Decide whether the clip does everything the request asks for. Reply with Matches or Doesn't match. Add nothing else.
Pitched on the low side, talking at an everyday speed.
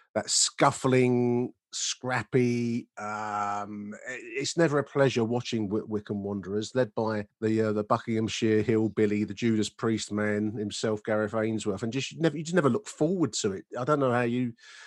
Matches